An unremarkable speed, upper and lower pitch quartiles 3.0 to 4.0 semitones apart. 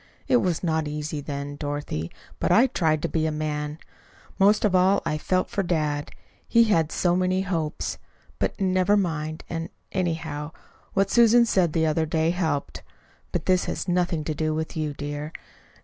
Yes: average, 175 wpm; average, 3.4 semitones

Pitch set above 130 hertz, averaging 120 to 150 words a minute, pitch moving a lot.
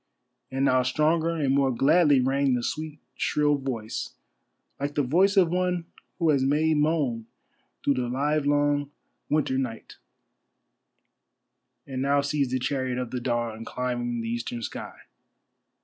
No: medium, 140 Hz; average, 140 wpm; average, 3.0 semitones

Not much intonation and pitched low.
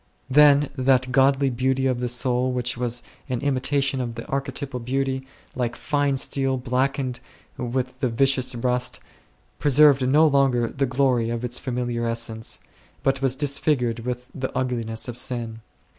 Yes: narrow, 1.9 semitones; low, 130 Hz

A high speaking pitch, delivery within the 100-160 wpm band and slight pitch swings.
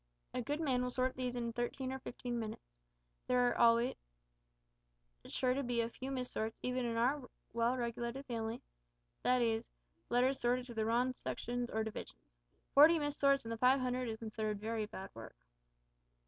No: high, 245 Hz; average, 180 wpm; narrow, 2.0 semitones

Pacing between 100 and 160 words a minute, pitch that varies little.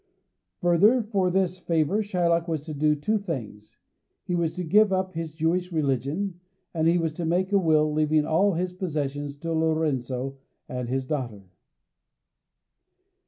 No: average, 155 wpm; average, 3.5 semitones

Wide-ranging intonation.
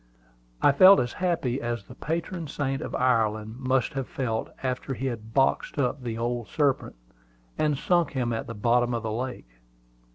No: average, 3.2 semitones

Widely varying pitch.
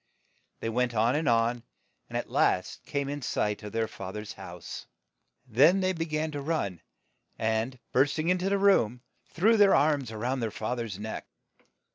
Yes: wide, 6.0 semitones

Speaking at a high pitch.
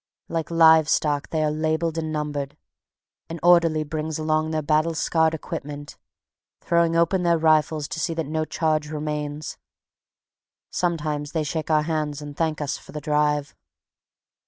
No: medium, 155 Hz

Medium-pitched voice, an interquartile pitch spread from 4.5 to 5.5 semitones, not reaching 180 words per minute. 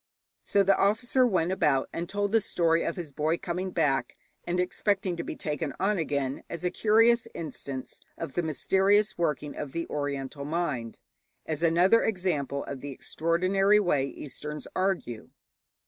Yes: medium, 170 Hz; average, 4.8 semitones; average, 160 wpm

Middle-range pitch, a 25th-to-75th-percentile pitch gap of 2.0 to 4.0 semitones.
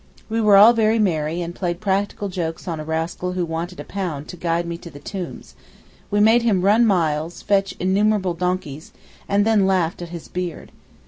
Yes: medium, 180 Hz; average, 3.3 semitones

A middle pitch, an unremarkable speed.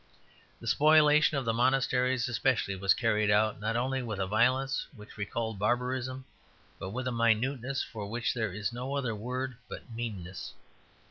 No: low, 120 Hz; average, 160 wpm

